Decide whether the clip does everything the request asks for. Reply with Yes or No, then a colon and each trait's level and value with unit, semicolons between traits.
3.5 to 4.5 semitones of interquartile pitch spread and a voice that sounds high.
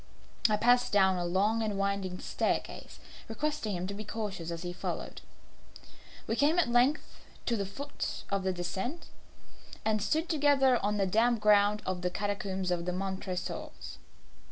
Yes: average, 4.1 semitones; high, 205 Hz